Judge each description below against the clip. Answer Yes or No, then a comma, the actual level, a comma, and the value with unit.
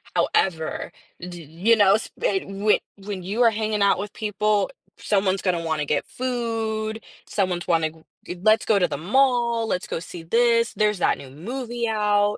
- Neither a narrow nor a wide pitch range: Yes, average, 3.8 semitones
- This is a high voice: Yes, high, 205 Hz